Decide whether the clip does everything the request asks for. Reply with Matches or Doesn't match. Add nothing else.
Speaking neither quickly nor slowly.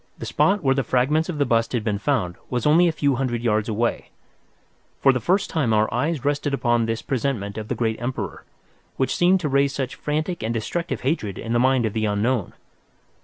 Doesn't match